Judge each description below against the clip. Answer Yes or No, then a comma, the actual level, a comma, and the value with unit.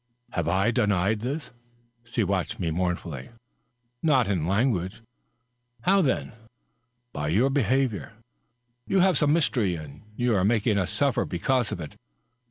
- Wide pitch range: Yes, wide, 5.8 semitones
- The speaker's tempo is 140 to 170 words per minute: Yes, average, 150 wpm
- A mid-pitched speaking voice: No, low, 110 Hz